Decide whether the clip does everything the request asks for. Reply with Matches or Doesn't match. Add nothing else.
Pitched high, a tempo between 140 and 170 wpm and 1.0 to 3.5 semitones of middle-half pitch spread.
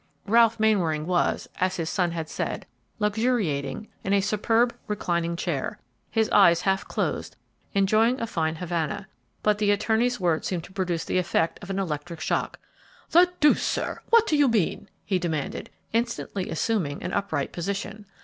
Doesn't match